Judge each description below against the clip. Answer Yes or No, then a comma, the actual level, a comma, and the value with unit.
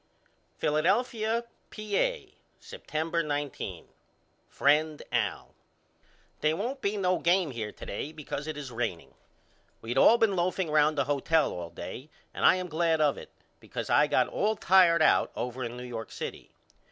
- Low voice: No, medium, 155 Hz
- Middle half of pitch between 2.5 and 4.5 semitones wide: No, average, 5.3 semitones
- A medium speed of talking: Yes, average, 155 wpm